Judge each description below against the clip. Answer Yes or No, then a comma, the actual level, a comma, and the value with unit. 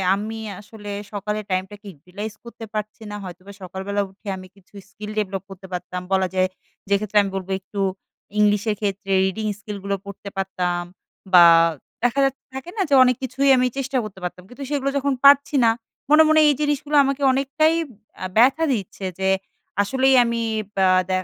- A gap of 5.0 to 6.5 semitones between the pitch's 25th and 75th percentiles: Yes, wide, 5.5 semitones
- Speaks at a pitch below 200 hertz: No, high, 210 Hz